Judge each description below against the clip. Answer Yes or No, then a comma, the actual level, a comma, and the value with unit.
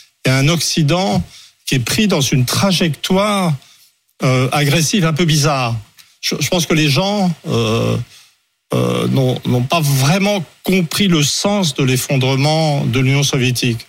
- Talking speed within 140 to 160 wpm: Yes, slow, 145 wpm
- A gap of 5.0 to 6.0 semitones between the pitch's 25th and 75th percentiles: Yes, wide, 5.4 semitones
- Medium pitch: Yes, medium, 150 Hz